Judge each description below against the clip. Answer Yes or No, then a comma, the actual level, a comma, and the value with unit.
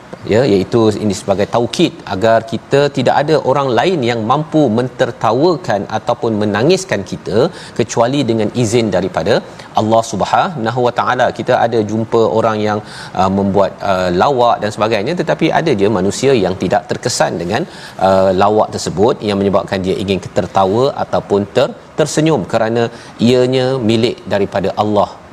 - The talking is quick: Yes, fast, 140 wpm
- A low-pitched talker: Yes, low, 115 Hz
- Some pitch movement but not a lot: Yes, average, 3.6 semitones